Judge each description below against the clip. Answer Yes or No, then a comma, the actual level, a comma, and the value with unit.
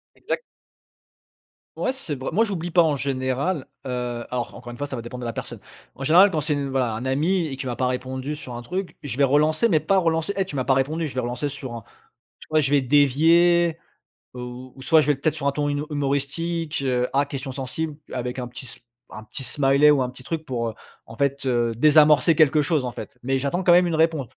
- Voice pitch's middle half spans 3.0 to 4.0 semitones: Yes, average, 3.7 semitones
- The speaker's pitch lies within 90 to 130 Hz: No, medium, 140 Hz